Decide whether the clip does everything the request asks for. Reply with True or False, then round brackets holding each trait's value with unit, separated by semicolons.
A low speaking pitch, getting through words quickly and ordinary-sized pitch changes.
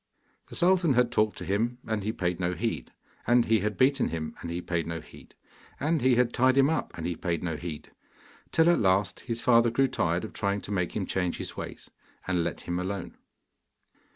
False (100 Hz; 215 wpm; 5.8 semitones)